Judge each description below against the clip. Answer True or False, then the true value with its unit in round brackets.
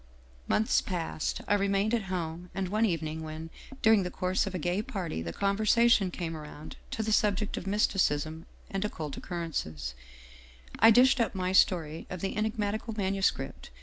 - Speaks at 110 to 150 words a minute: False (175 wpm)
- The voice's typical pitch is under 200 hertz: True (190 Hz)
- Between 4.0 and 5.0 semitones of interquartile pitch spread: True (4.5 semitones)